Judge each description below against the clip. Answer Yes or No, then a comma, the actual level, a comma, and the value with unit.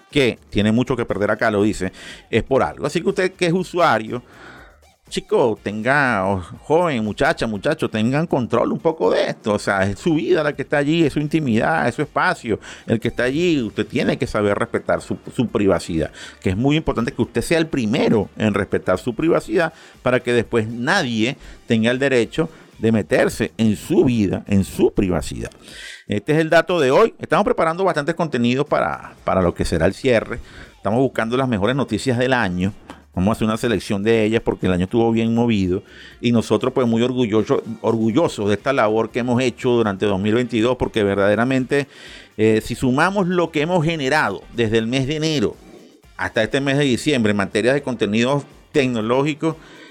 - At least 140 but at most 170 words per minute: No, fast, 190 wpm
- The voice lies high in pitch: No, low, 120 Hz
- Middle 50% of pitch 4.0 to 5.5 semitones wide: Yes, average, 4.8 semitones